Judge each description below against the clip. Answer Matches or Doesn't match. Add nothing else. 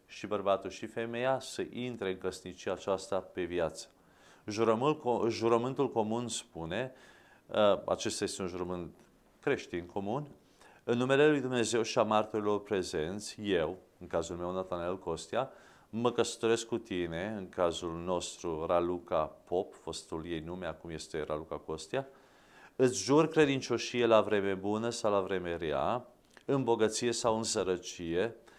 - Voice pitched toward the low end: Matches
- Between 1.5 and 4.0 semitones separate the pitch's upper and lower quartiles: Doesn't match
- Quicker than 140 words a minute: Doesn't match